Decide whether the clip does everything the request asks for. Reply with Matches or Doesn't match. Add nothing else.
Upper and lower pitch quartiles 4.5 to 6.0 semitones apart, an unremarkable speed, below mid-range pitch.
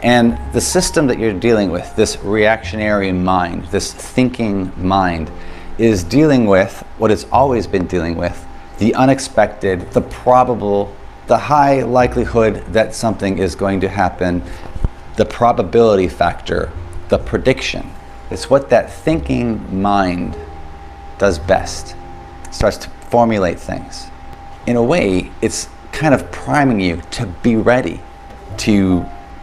Doesn't match